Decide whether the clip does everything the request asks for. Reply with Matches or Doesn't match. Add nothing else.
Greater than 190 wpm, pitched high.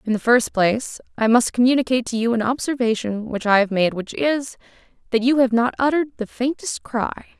Matches